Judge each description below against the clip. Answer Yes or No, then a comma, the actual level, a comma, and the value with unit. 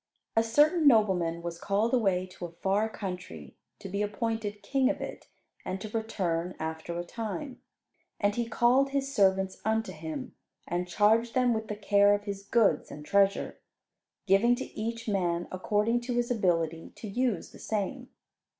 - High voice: Yes, high, 205 Hz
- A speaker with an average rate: Yes, average, 170 wpm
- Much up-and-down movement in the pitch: No, average, 4.1 semitones